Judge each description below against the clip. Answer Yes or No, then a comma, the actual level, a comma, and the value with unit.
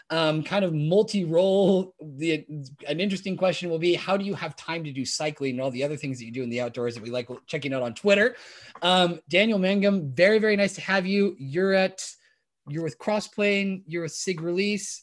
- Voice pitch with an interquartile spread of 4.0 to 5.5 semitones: Yes, average, 4.6 semitones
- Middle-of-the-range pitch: Yes, medium, 175 Hz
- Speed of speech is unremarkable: No, fast, 215 wpm